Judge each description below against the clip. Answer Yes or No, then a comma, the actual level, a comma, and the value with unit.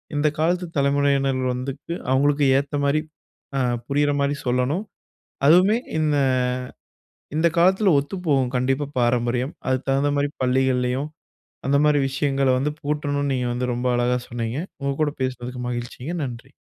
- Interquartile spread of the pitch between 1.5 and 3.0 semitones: Yes, narrow, 2.6 semitones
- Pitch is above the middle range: No, medium, 140 Hz